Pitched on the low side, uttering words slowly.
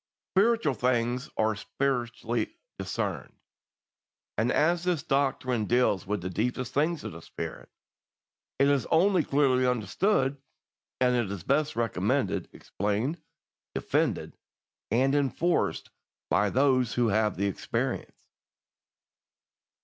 Yes: low, 130 Hz; slow, 110 wpm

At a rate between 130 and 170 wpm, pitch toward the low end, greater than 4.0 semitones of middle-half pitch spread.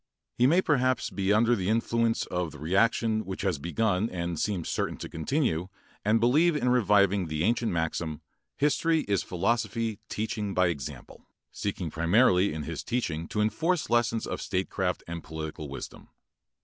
Yes: average, 160 wpm; low, 100 Hz; average, 5.3 semitones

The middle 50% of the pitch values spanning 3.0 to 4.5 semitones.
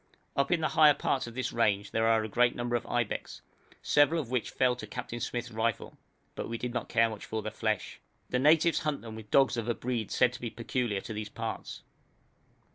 No: narrow, 2.4 semitones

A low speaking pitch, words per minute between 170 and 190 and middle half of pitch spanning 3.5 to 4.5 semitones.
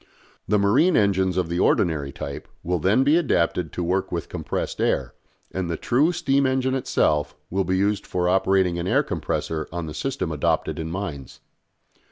Yes: very low, 95 Hz; average, 180 wpm; average, 4.2 semitones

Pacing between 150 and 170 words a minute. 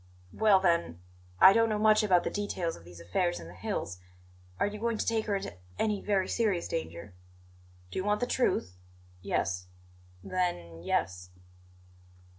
Yes: average, 165 wpm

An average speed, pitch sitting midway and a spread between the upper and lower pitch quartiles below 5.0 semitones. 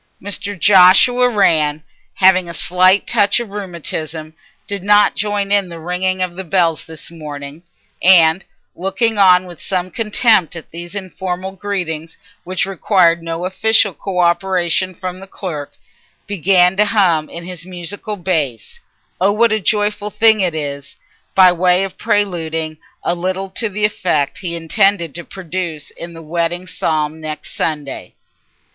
Yes: average, 150 wpm; medium, 180 Hz; average, 3.0 semitones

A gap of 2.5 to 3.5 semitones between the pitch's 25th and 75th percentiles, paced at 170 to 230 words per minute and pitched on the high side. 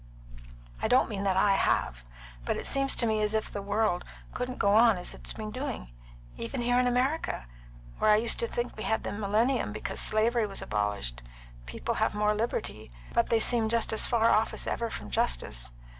Yes: average, 2.9 semitones; fast, 205 wpm; high, 220 Hz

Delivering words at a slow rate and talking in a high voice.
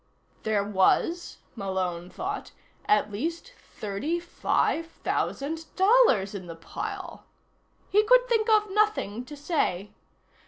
Yes: slow, 115 wpm; very high, 325 Hz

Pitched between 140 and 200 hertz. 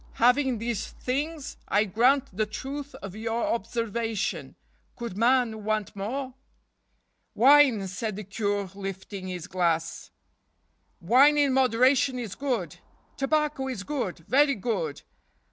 No: high, 230 Hz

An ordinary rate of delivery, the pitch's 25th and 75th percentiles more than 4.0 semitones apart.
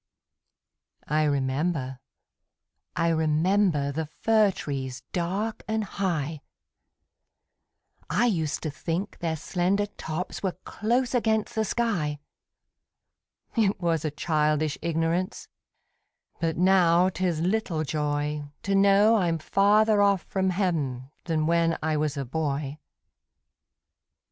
No: slow, 110 wpm; average, 4.5 semitones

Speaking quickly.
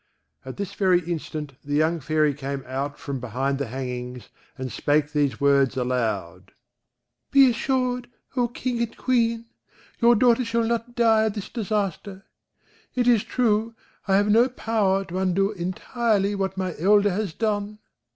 No: average, 155 wpm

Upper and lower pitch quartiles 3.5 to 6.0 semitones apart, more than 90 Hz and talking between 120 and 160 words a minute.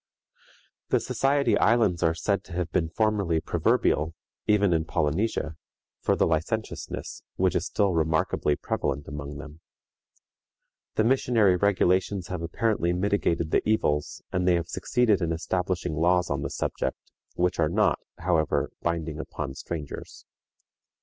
No: average, 4.2 semitones; very low, 85 Hz; average, 140 wpm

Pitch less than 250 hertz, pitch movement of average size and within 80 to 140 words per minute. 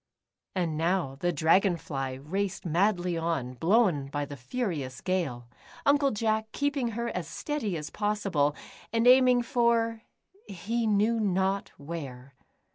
No: high, 190 Hz; wide, 6.9 semitones; slow, 135 wpm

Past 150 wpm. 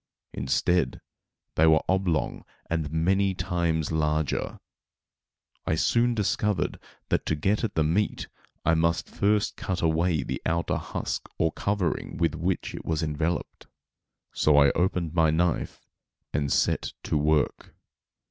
No: slow, 135 wpm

